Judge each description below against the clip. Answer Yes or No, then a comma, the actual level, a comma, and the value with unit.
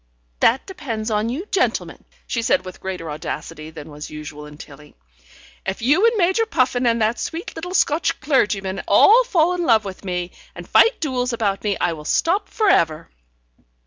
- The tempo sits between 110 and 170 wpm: No, average, 180 wpm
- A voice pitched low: No, high, 230 Hz